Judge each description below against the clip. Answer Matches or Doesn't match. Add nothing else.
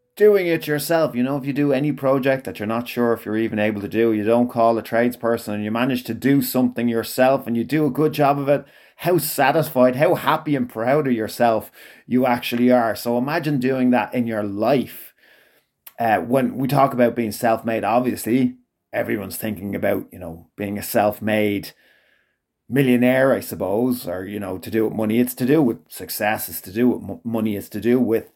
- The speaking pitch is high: Doesn't match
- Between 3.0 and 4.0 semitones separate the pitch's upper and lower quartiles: Matches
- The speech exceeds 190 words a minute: Matches